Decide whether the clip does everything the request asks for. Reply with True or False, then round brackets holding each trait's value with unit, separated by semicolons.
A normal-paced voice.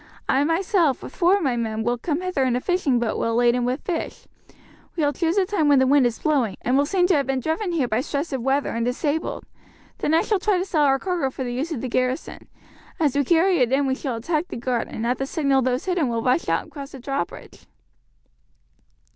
False (250 wpm)